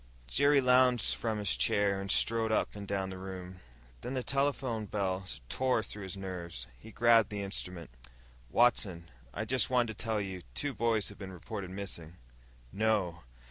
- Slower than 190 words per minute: Yes, average, 170 wpm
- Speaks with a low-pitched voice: Yes, low, 105 Hz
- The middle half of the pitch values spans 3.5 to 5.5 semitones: Yes, average, 3.8 semitones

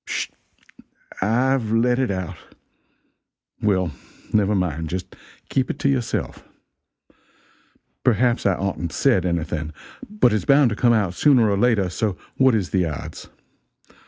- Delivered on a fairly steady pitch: No, average, 5.1 semitones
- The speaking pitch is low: Yes, low, 105 Hz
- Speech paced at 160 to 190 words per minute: No, slow, 135 wpm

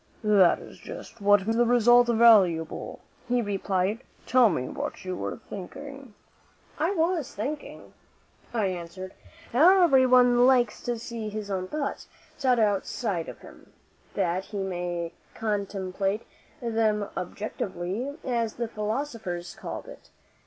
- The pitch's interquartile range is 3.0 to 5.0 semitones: Yes, average, 4.2 semitones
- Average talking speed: No, slow, 130 wpm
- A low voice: No, high, 215 Hz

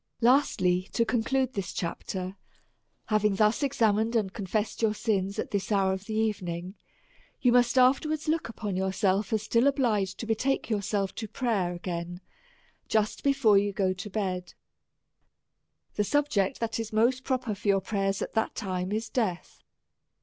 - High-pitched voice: Yes, high, 210 Hz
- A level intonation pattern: No, average, 3.3 semitones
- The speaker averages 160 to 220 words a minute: Yes, average, 165 wpm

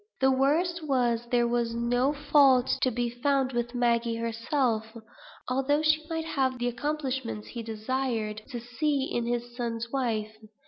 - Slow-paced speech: No, average, 150 wpm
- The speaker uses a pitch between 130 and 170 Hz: No, high, 245 Hz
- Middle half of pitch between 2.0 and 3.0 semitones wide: Yes, average, 2.7 semitones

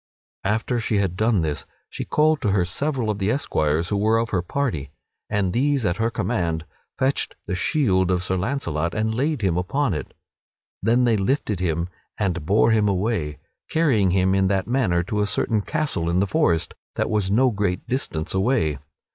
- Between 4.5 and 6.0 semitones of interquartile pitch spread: Yes, average, 4.9 semitones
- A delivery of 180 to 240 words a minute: Yes, average, 190 wpm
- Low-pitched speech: Yes, low, 100 Hz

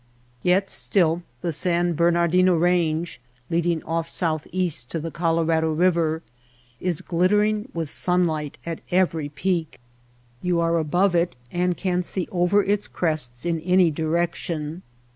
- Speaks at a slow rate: Yes, slow, 130 wpm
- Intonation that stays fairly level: Yes, narrow, 1.9 semitones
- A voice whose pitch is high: No, medium, 170 Hz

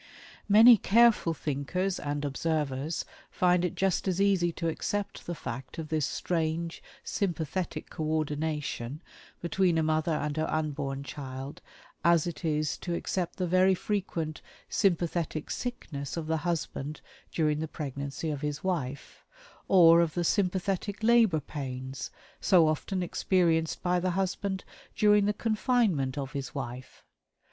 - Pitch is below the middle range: No, medium, 165 Hz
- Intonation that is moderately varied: Yes, average, 3.9 semitones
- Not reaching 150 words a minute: Yes, average, 140 wpm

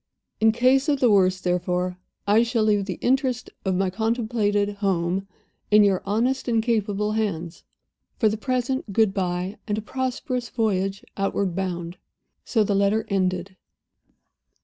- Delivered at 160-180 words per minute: No, average, 150 wpm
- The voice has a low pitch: No, high, 205 Hz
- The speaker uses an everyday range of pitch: Yes, average, 3.4 semitones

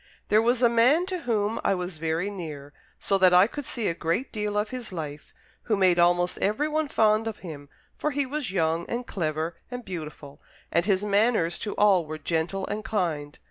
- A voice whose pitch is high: Yes, high, 195 Hz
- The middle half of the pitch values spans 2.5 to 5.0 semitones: No, wide, 5.5 semitones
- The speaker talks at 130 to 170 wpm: No, average, 200 wpm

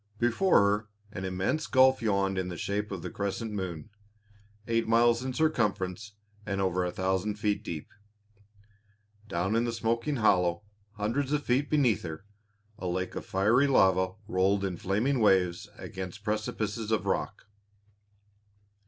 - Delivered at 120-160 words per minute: Yes, average, 145 wpm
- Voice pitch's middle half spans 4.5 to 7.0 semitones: No, average, 3.7 semitones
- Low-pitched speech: Yes, low, 105 Hz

